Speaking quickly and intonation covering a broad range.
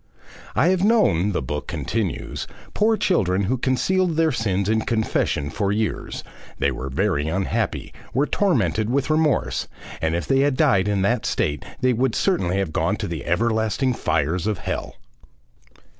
No: average, 160 wpm; wide, 7.2 semitones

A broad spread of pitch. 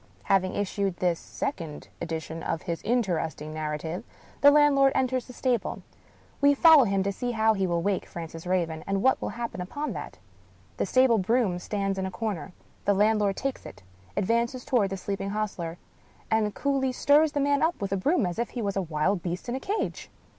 Yes: wide, 6.1 semitones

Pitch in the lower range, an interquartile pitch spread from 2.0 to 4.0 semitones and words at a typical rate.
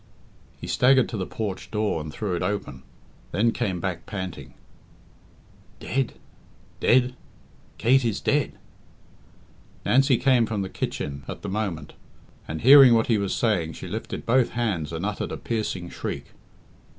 No: low, 105 Hz; average, 4.7 semitones; average, 150 wpm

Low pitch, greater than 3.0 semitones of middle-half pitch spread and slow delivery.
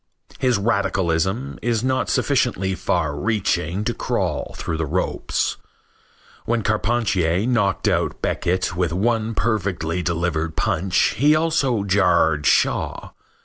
Yes: very low, 95 Hz; average, 5.1 semitones; slow, 115 wpm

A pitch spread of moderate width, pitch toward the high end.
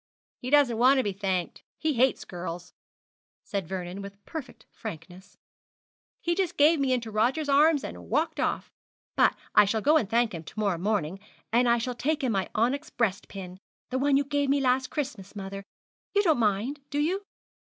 No: wide, 6.4 semitones; high, 235 Hz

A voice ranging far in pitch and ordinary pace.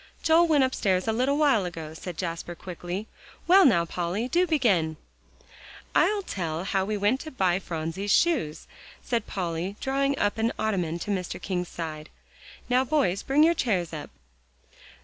Yes: wide, 7.5 semitones; average, 160 wpm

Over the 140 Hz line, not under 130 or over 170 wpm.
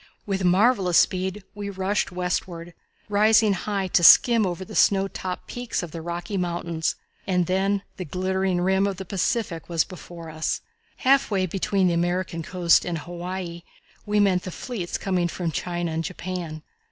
Yes: medium, 185 Hz; average, 165 wpm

